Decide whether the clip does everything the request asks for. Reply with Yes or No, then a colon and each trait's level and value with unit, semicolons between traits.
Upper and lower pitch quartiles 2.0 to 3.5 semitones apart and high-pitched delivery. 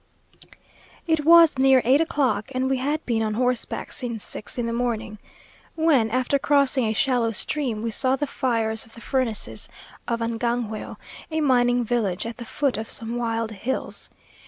Yes: average, 2.9 semitones; high, 245 Hz